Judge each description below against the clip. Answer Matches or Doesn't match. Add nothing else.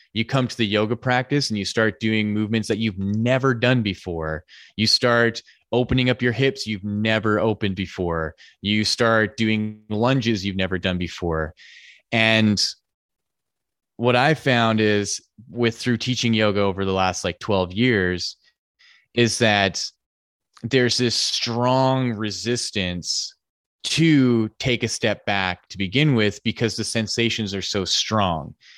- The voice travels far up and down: Doesn't match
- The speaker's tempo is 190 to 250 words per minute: Doesn't match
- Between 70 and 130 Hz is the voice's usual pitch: Matches